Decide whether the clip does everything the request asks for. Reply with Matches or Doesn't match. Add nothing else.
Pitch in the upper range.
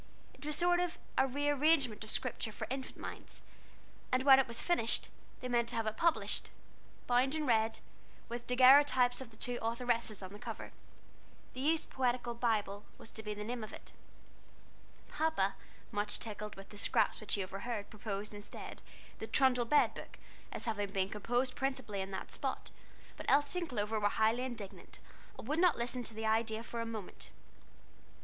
Matches